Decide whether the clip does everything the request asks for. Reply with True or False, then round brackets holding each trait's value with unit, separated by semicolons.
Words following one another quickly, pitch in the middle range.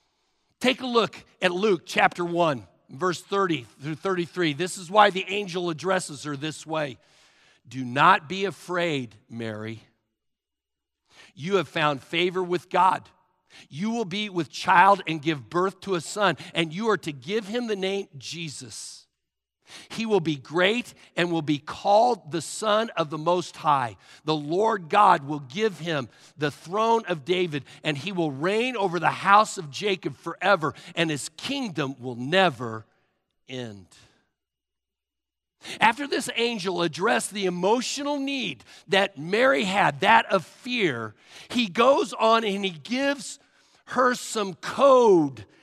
False (150 wpm; 180 Hz)